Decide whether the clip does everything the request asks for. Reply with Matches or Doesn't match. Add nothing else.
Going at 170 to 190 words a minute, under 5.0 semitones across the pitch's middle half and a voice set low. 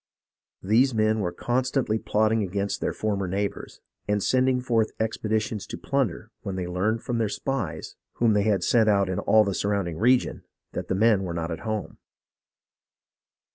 Matches